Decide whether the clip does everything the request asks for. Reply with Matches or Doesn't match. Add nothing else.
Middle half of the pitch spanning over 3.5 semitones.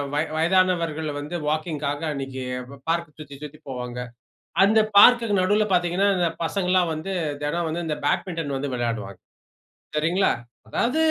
Matches